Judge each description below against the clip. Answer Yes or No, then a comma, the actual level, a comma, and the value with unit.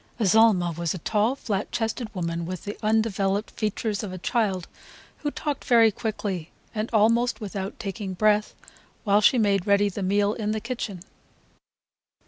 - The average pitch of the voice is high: Yes, high, 210 Hz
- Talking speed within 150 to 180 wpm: Yes, average, 155 wpm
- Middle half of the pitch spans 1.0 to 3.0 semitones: Yes, narrow, 2.5 semitones